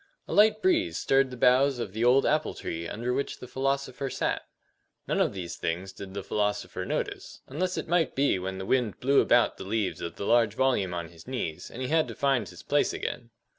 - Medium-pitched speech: No, low, 125 Hz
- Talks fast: Yes, fast, 220 wpm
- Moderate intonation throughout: No, wide, 6.0 semitones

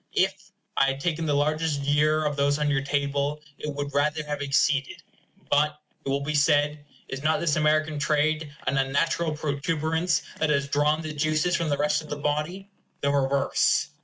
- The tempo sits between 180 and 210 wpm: Yes, average, 185 wpm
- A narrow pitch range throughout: Yes, narrow, 1.5 semitones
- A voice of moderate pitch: Yes, medium, 150 Hz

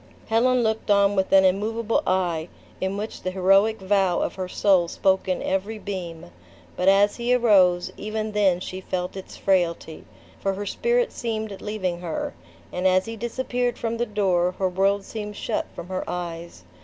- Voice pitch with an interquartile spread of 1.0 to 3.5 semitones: Yes, average, 2.9 semitones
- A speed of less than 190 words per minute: Yes, average, 175 wpm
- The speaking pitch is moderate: No, high, 195 Hz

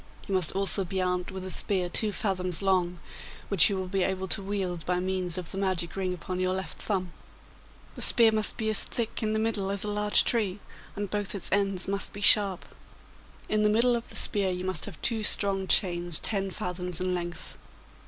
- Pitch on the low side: No, high, 190 Hz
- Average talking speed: No, fast, 210 wpm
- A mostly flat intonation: Yes, narrow, 2.2 semitones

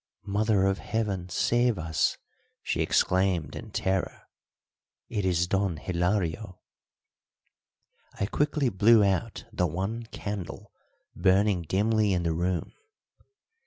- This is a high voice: No, very low, 95 Hz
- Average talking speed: No, slow, 110 wpm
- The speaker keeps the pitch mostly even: No, average, 3.2 semitones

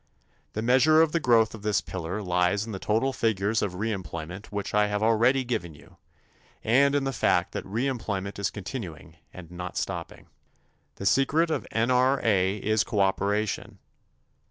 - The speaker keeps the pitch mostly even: No, average, 4.4 semitones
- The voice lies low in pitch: Yes, low, 105 Hz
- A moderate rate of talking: Yes, average, 155 wpm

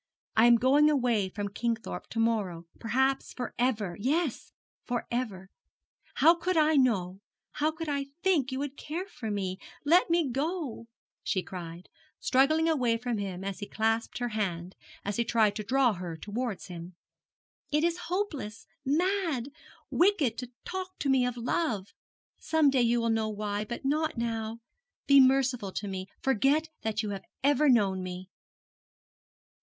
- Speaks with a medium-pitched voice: No, high, 240 Hz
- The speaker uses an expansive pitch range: Yes, wide, 5.8 semitones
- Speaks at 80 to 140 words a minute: No, average, 160 wpm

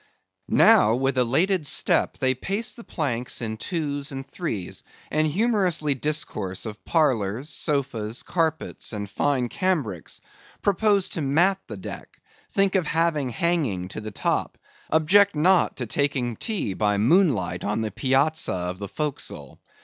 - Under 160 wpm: Yes, average, 140 wpm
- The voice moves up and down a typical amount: No, wide, 7.2 semitones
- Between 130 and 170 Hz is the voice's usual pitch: Yes, medium, 140 Hz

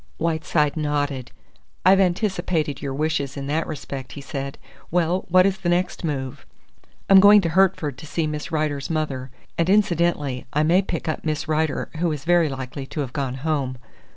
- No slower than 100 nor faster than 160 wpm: No, average, 180 wpm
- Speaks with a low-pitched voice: No, medium, 155 Hz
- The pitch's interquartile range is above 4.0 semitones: No, average, 3.6 semitones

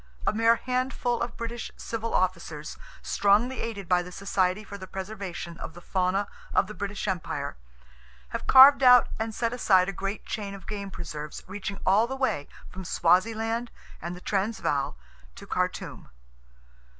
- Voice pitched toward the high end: Yes, high, 200 Hz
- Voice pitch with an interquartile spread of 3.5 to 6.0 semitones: Yes, average, 3.8 semitones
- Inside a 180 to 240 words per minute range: No, average, 160 wpm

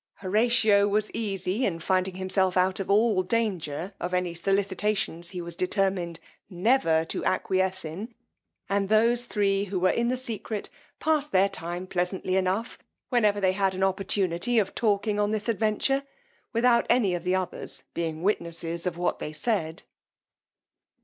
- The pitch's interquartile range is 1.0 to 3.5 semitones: Yes, average, 2.9 semitones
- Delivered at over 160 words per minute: No, average, 155 wpm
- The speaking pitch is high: Yes, high, 195 Hz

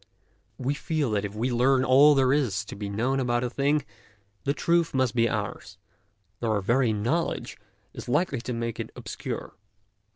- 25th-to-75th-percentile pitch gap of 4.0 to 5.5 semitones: No, average, 3.5 semitones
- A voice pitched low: Yes, low, 125 Hz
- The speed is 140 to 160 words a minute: No, average, 185 wpm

